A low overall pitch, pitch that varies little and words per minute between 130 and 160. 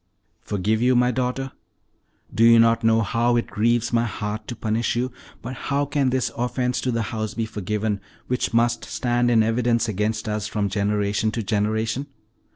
No: low, 115 Hz; narrow, 2.2 semitones; average, 175 wpm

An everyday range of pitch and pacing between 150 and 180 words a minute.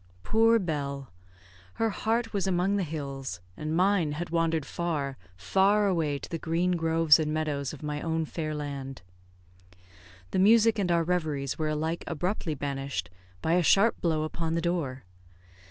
Yes: average, 3.5 semitones; average, 160 wpm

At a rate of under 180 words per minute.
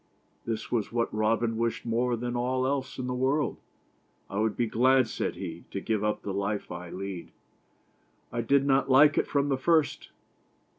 No: average, 195 wpm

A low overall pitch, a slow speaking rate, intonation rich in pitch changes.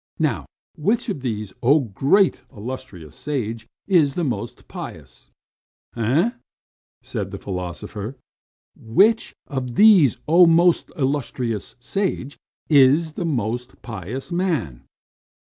Yes: low, 130 Hz; slow, 110 wpm; wide, 6.7 semitones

